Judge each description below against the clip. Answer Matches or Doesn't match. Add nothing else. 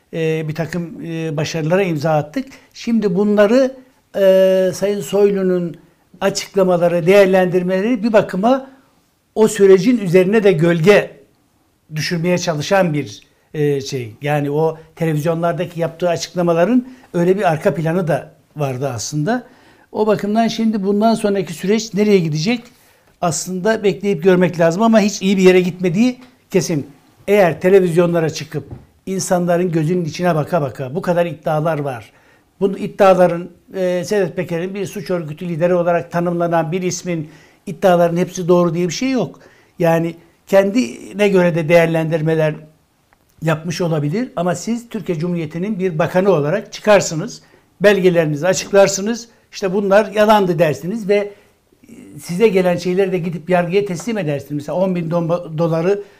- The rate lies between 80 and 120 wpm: Doesn't match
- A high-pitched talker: Doesn't match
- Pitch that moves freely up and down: Doesn't match